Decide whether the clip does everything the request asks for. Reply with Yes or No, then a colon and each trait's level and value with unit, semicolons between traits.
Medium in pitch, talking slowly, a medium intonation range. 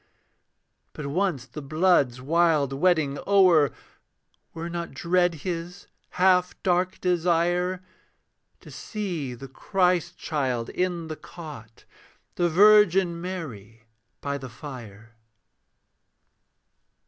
Yes: medium, 170 Hz; slow, 100 wpm; average, 4.5 semitones